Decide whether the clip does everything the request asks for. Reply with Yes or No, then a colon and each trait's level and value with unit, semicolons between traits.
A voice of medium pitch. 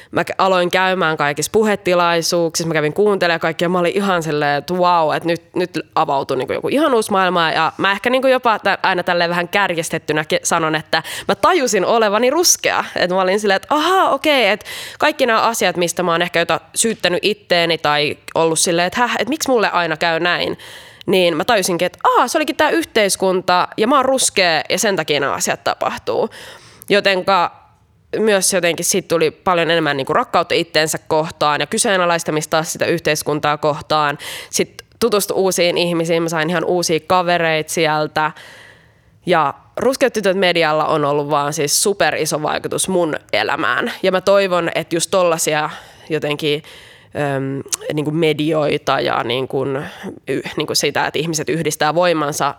Yes: medium, 175 Hz